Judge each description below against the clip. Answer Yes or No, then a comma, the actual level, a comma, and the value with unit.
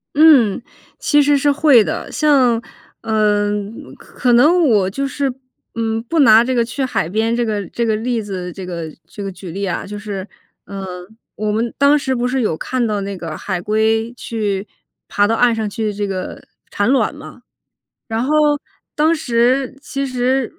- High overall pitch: Yes, high, 225 Hz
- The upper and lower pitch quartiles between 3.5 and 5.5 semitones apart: Yes, average, 4.2 semitones